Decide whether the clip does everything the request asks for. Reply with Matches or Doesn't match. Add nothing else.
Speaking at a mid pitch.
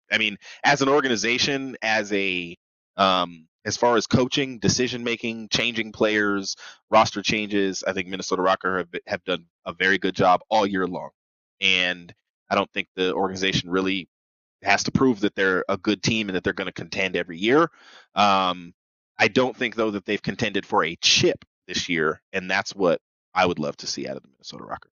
Doesn't match